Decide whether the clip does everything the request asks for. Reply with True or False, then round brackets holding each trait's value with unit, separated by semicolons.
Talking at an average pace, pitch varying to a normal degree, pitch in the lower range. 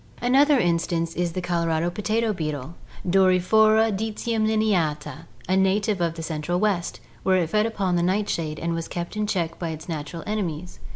False (165 wpm; 4.2 semitones; 180 Hz)